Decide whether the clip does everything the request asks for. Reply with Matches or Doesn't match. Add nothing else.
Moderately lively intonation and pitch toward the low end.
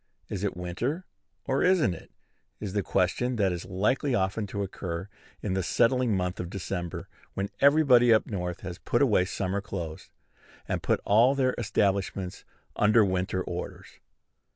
Matches